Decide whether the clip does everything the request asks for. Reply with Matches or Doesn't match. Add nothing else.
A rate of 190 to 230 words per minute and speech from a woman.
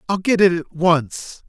Doesn't match